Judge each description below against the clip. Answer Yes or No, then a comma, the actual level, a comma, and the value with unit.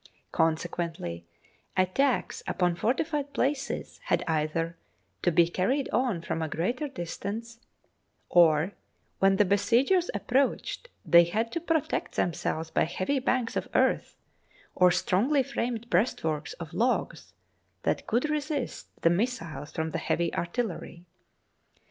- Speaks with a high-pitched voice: Yes, high, 195 Hz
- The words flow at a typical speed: No, slow, 125 wpm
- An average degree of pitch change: No, wide, 7.2 semitones